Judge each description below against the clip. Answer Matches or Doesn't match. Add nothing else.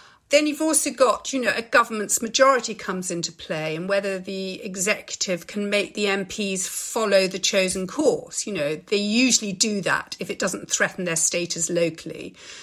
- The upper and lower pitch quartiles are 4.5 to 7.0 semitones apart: Doesn't match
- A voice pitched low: Doesn't match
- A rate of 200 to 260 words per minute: Doesn't match